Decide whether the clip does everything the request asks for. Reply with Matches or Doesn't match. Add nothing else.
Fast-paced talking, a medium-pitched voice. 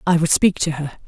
Matches